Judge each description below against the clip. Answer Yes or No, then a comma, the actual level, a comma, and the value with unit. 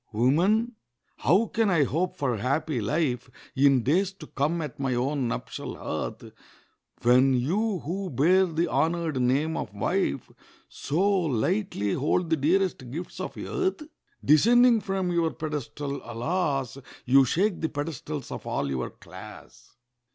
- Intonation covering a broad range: Yes, wide, 5.7 semitones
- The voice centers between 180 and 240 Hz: No, medium, 155 Hz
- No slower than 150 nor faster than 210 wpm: No, average, 140 wpm